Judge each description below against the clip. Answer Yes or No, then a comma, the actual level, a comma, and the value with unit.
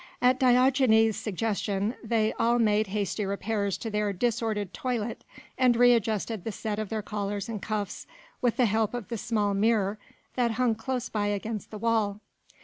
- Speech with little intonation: Yes, narrow, 2.2 semitones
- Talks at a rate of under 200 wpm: Yes, average, 170 wpm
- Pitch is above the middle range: Yes, high, 220 Hz